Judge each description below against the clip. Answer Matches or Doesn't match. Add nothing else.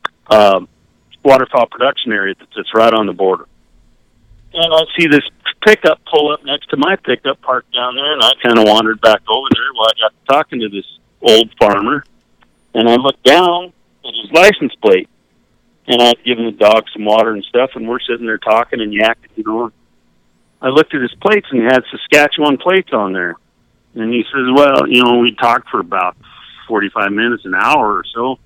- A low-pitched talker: Matches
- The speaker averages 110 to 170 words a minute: Doesn't match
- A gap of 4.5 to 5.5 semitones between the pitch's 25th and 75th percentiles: Matches